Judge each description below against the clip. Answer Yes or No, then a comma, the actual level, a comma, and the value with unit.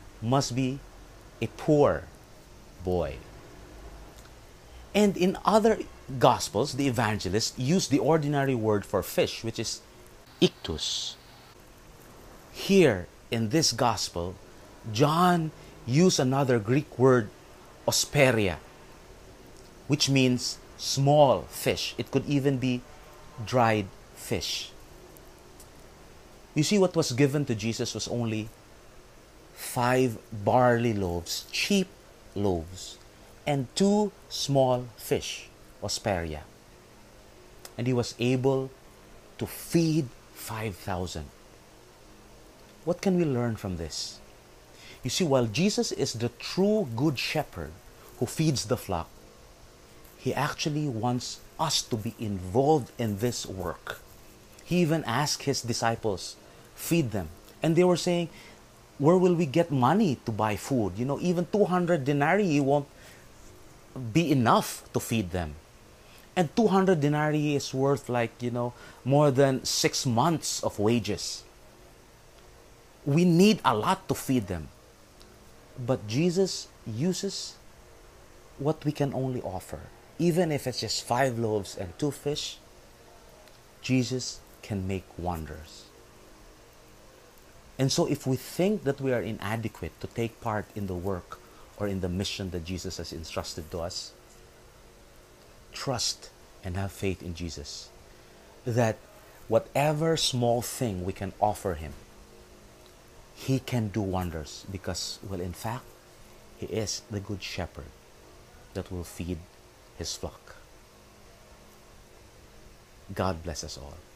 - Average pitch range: No, wide, 6.2 semitones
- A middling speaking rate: No, slow, 120 wpm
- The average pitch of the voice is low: Yes, low, 120 Hz